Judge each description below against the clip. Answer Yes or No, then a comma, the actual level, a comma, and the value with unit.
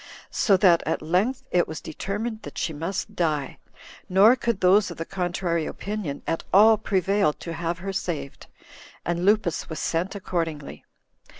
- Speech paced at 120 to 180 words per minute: Yes, average, 160 wpm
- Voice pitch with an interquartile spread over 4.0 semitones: No, average, 3.4 semitones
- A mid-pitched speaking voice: Yes, medium, 180 Hz